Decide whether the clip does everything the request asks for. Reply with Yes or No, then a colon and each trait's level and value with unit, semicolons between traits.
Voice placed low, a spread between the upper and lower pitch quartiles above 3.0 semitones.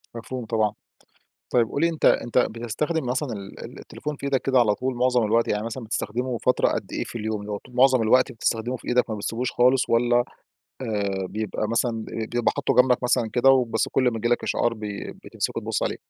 No: low, 120 Hz; narrow, 2.5 semitones